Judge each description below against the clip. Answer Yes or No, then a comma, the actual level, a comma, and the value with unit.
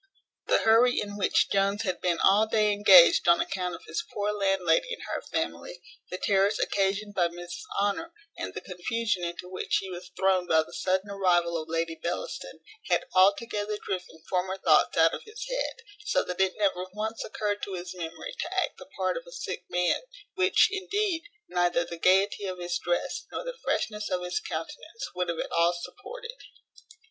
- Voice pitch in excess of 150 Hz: Yes, high, 190 Hz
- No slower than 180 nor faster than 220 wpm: Yes, average, 190 wpm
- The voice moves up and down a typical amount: Yes, average, 3.2 semitones